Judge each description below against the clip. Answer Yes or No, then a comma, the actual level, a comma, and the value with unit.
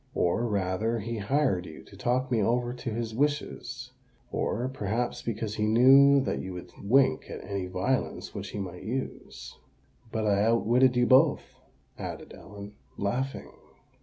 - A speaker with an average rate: Yes, average, 150 wpm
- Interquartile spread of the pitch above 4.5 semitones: No, average, 4.1 semitones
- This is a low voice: Yes, low, 115 Hz